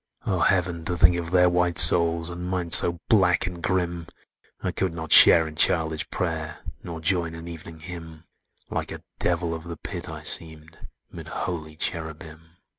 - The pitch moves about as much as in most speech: No, narrow, 1.5 semitones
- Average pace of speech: Yes, average, 175 wpm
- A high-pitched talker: No, very low, 85 Hz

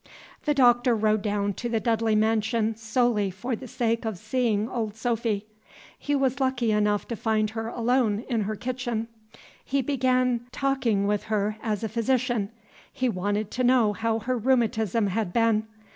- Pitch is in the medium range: No, high, 225 Hz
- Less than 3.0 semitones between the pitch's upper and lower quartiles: Yes, narrow, 2.6 semitones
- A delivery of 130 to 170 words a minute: Yes, average, 165 wpm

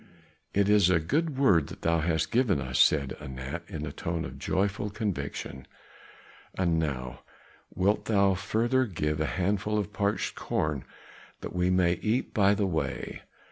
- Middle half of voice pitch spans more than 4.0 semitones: Yes, average, 4.9 semitones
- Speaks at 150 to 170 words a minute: Yes, average, 165 wpm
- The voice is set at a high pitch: No, very low, 90 Hz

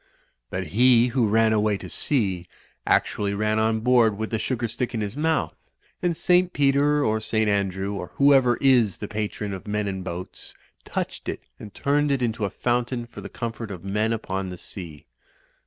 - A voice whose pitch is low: Yes, low, 110 Hz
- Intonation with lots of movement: No, average, 3.7 semitones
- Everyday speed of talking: Yes, average, 190 wpm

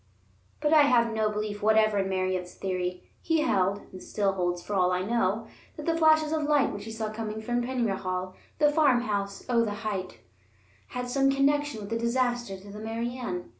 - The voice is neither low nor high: No, high, 220 Hz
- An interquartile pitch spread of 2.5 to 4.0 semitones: No, average, 4.5 semitones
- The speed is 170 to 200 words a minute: Yes, average, 195 wpm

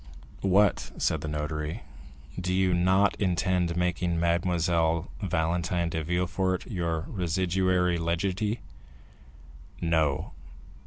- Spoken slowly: Yes, slow, 95 wpm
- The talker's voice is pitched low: Yes, very low, 90 Hz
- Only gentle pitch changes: Yes, narrow, 1.9 semitones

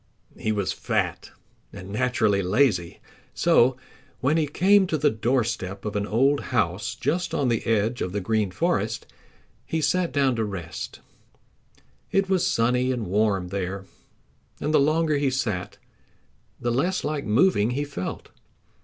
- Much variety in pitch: Yes, wide, 5.9 semitones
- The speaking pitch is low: Yes, low, 120 Hz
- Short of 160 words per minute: Yes, average, 150 wpm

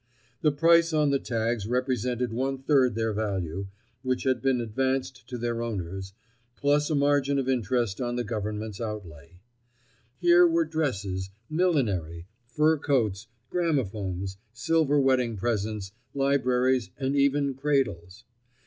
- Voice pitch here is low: Yes, low, 125 Hz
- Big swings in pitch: No, average, 4.9 semitones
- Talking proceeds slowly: Yes, slow, 130 wpm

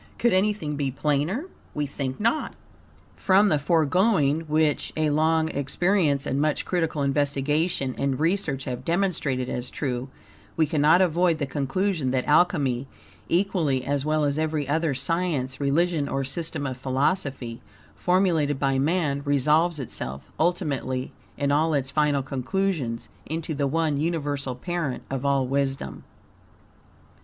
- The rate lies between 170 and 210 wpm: No, slow, 135 wpm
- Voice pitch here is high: No, medium, 145 Hz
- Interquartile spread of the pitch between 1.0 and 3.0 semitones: No, average, 3.4 semitones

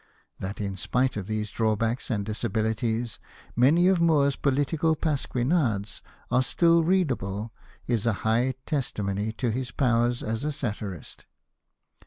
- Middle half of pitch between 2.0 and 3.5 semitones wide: No, average, 4.6 semitones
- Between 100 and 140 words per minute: Yes, slow, 135 wpm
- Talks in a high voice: No, low, 120 Hz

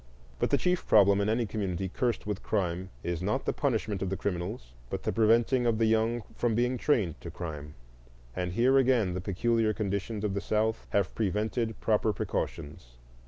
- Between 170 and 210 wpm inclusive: Yes, average, 185 wpm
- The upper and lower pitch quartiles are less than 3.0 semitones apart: No, average, 3.5 semitones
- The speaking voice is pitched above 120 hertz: No, low, 105 Hz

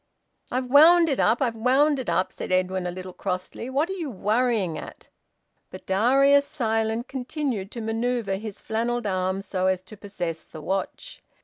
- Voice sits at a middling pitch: No, high, 225 Hz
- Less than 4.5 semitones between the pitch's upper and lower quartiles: No, wide, 5.5 semitones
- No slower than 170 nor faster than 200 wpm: Yes, average, 175 wpm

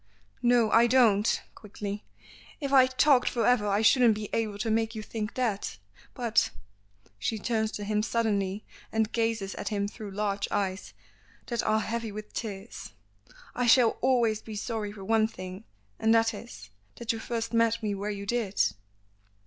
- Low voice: No, high, 220 Hz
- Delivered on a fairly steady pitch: Yes, narrow, 2.2 semitones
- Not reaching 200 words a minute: Yes, average, 175 wpm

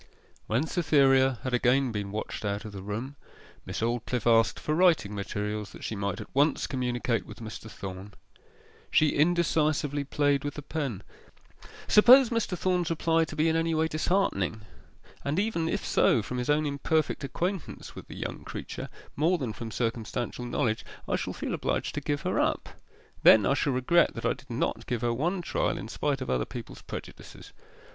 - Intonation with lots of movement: Yes, wide, 6.0 semitones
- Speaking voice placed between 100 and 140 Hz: Yes, low, 135 Hz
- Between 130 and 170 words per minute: No, average, 185 wpm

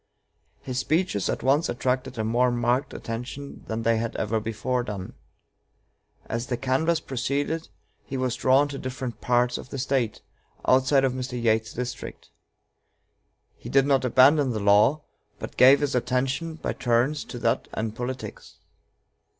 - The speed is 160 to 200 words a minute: No, average, 150 wpm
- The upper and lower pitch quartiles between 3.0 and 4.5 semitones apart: No, narrow, 2.6 semitones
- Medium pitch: No, low, 125 Hz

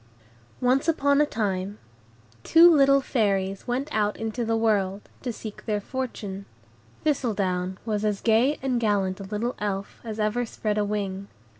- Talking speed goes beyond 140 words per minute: Yes, average, 155 wpm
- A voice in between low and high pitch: No, high, 215 Hz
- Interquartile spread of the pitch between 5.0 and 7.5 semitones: No, average, 3.7 semitones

